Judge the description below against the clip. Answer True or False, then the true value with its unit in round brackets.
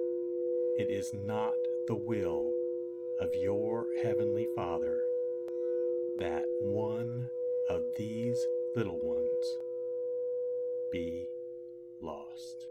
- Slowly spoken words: True (80 wpm)